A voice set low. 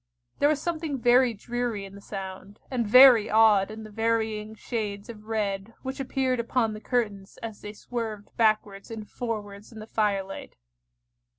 No: high, 220 Hz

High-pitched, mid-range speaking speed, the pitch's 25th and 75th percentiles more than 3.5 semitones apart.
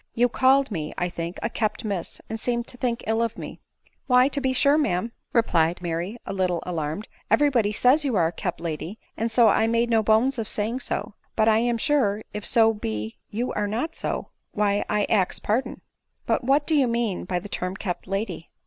No: high, 220 Hz; fast, 230 wpm; average, 4.6 semitones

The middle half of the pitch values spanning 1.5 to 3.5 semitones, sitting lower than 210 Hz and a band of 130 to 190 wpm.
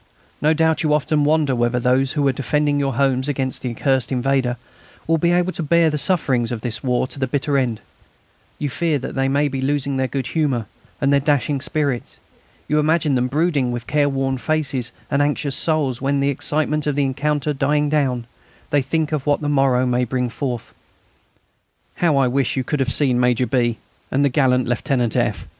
No: average, 2.7 semitones; medium, 140 Hz; average, 200 wpm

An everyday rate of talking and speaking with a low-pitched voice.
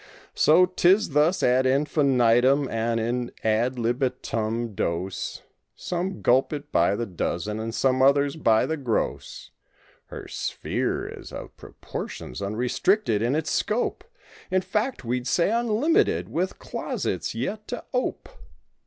No: slow, 130 wpm; low, 130 Hz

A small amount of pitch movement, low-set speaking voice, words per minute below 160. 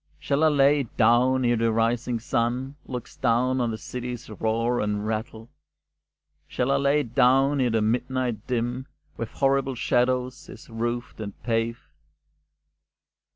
Yes: narrow, 2.2 semitones; low, 120 Hz; average, 150 wpm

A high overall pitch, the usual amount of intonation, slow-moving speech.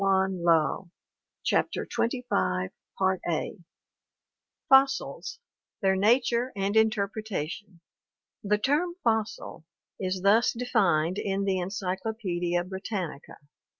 Yes: high, 195 Hz; average, 3.5 semitones; slow, 85 wpm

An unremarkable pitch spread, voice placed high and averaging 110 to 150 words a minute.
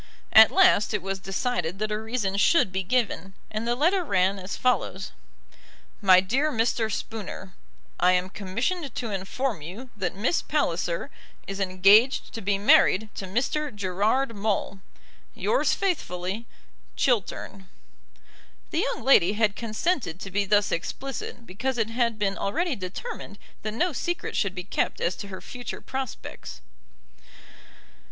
Yes: average, 4.7 semitones; high, 210 Hz; average, 145 wpm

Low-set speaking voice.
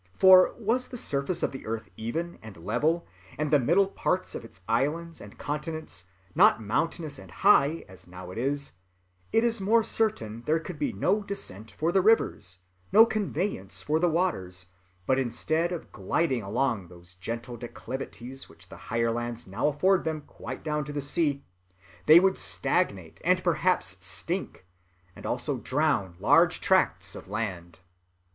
No: medium, 145 Hz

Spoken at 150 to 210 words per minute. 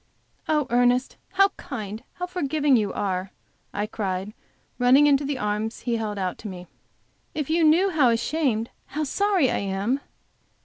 Yes: average, 160 wpm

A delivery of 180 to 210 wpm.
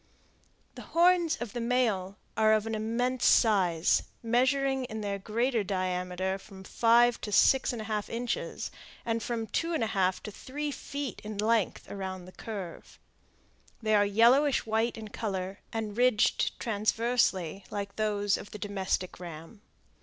No: average, 155 wpm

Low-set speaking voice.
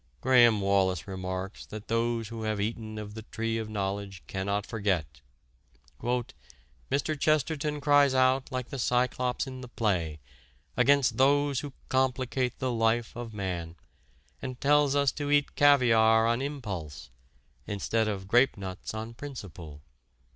Yes: low, 115 Hz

